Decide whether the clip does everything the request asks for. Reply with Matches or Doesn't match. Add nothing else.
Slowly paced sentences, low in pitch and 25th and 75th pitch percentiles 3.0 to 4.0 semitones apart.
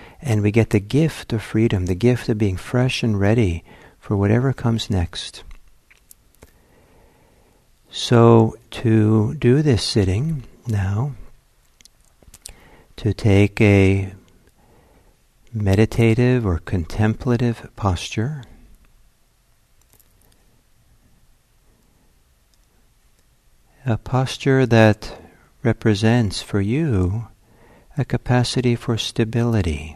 Matches